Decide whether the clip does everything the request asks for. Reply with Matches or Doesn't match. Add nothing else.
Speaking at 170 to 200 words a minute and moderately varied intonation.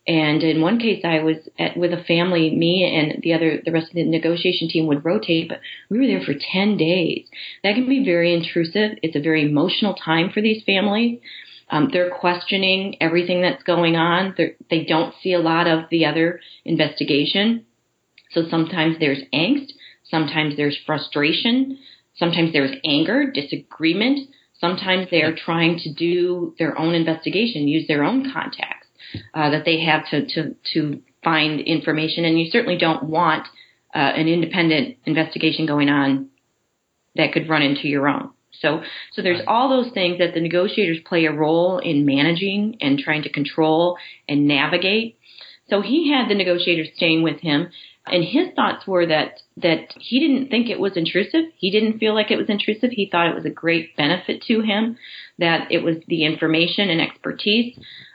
Matches